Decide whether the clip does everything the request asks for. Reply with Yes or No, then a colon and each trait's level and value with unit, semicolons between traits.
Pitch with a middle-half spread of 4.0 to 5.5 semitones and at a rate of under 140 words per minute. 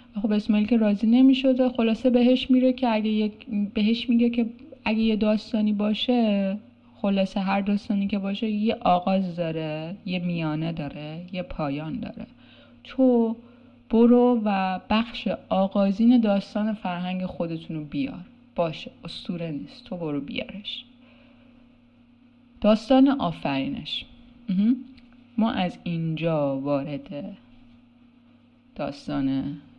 Yes: average, 5.0 semitones; average, 110 wpm